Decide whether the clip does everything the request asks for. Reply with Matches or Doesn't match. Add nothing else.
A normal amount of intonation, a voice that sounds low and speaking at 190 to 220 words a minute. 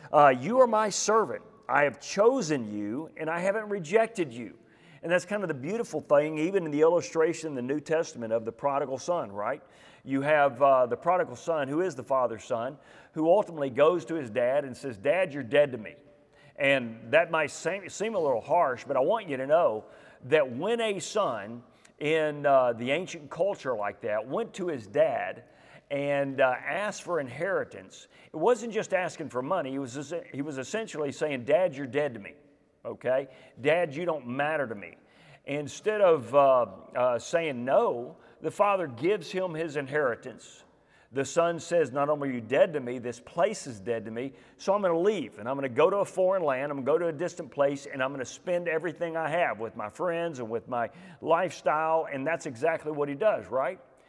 Doesn't match